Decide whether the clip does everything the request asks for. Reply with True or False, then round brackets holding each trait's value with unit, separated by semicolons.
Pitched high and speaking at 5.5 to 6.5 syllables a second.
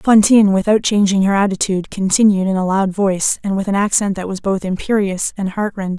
True (195 Hz; 5.9 syllables/s)